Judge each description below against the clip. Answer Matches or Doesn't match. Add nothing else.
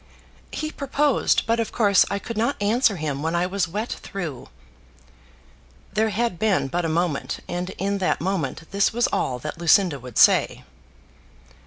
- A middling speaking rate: Matches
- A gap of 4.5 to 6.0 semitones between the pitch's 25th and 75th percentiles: Matches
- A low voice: Doesn't match